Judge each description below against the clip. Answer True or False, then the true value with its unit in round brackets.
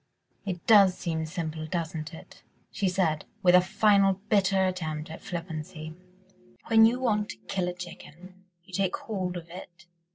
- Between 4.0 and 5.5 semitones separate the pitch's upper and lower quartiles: False (3.1 semitones)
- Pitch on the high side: False (180 Hz)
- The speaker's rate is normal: True (160 wpm)